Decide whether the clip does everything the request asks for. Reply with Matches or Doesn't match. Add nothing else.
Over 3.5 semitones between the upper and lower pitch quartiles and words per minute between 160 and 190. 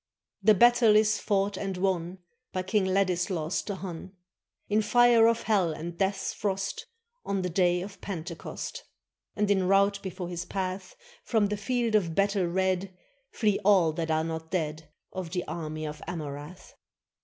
Doesn't match